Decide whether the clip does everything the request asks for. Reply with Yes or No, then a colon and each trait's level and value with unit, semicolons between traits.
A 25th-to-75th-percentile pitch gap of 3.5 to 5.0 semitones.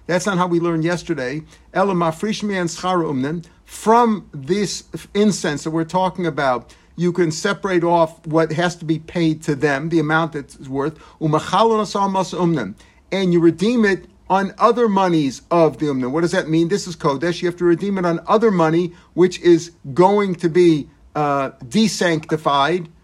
No: average, 2.7 semitones